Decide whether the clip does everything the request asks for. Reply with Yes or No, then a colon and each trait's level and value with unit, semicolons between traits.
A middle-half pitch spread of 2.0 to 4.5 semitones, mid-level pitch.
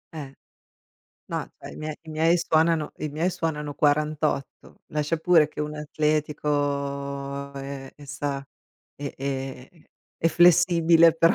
Yes: narrow, 2.5 semitones; medium, 150 Hz